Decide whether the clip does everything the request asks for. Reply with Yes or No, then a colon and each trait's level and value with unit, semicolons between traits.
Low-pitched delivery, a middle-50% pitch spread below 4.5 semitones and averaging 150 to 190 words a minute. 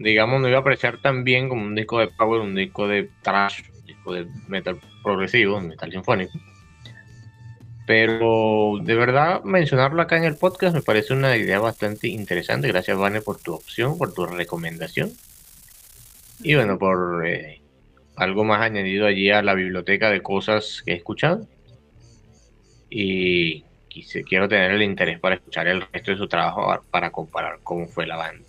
Yes: low, 105 Hz; average, 3.3 semitones; average, 165 wpm